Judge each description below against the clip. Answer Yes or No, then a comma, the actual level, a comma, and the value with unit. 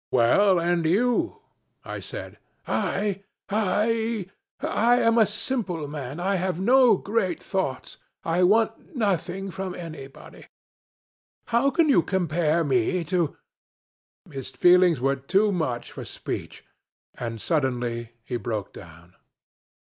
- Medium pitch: Yes, medium, 180 Hz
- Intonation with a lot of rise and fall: Yes, wide, 7.2 semitones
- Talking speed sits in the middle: No, slow, 125 wpm